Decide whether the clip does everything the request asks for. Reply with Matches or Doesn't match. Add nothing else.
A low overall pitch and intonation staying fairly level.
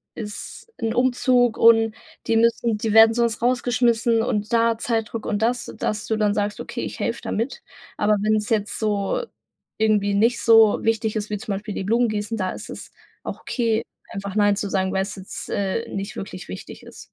Doesn't match